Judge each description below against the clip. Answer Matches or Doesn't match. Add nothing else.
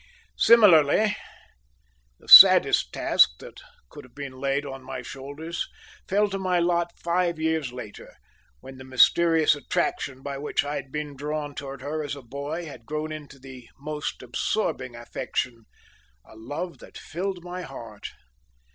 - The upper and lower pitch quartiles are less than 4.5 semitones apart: Matches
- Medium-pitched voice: Matches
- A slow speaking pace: Doesn't match